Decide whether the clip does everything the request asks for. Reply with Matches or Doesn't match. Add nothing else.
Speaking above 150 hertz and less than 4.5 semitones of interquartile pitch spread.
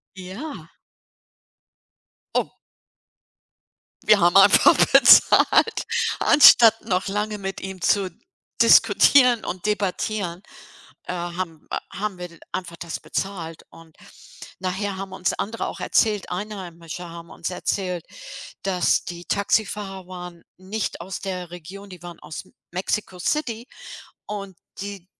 Matches